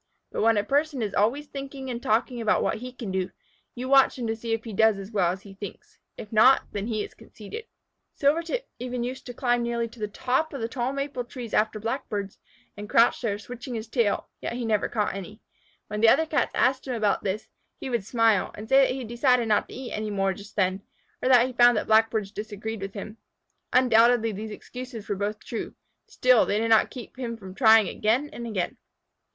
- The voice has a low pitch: No, high, 230 Hz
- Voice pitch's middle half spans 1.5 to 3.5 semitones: Yes, average, 3.1 semitones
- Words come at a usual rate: No, fast, 225 wpm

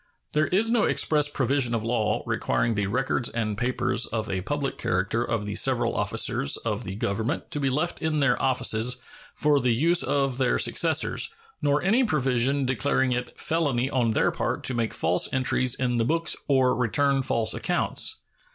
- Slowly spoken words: No, average, 180 wpm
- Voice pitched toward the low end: Yes, low, 130 Hz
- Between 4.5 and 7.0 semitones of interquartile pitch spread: No, average, 3.6 semitones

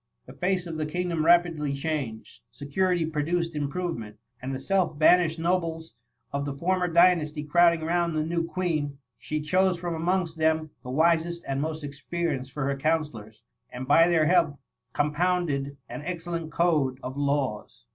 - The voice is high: No, medium, 160 Hz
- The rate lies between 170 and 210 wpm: No, average, 155 wpm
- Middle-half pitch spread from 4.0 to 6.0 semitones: No, average, 3.3 semitones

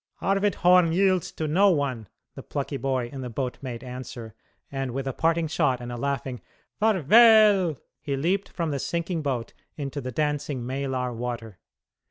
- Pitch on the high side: No, medium, 140 Hz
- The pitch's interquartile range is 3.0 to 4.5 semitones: No, average, 5.0 semitones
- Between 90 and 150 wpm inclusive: No, average, 170 wpm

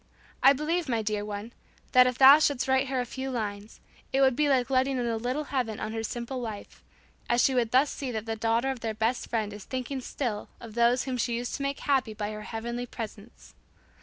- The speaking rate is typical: No, fast, 230 wpm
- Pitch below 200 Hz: No, high, 245 Hz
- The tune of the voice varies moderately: Yes, average, 3.0 semitones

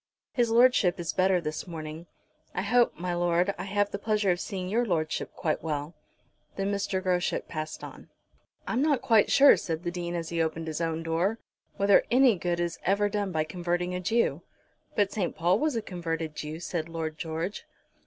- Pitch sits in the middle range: Yes, medium, 180 Hz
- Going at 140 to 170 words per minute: No, average, 195 wpm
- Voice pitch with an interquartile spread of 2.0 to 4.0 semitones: Yes, average, 3.7 semitones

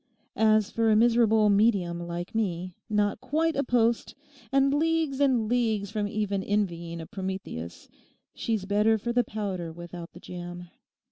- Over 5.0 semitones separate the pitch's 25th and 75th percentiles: No, average, 4.4 semitones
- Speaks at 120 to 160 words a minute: Yes, average, 150 wpm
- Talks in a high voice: Yes, high, 210 Hz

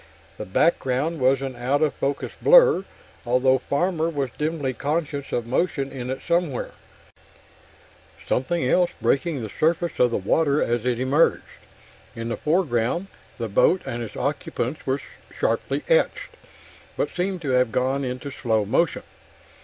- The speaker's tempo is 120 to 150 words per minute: Yes, average, 145 wpm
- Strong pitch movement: No, average, 4.7 semitones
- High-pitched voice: No, low, 135 Hz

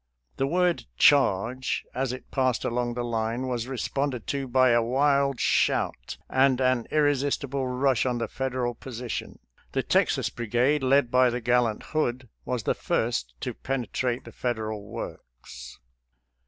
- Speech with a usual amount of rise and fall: No, narrow, 2.2 semitones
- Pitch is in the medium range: No, low, 125 Hz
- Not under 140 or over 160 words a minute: Yes, average, 155 wpm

